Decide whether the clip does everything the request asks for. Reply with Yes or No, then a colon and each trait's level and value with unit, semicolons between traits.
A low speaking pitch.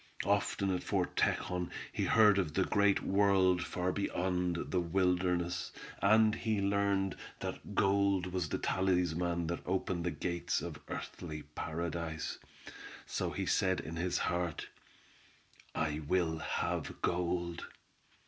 Yes: very low, 90 Hz